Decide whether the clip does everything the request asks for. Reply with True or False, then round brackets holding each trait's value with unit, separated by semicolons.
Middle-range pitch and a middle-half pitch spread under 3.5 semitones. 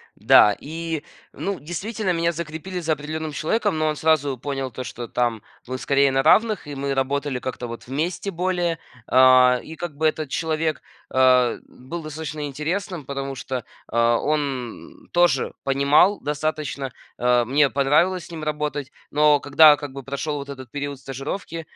True (145 Hz; 3.1 semitones)